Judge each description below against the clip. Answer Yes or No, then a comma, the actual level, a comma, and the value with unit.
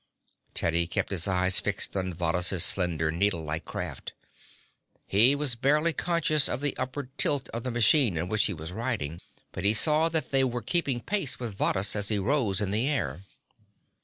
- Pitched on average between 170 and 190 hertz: No, low, 105 Hz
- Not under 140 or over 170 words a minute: No, average, 180 wpm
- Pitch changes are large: Yes, wide, 6.9 semitones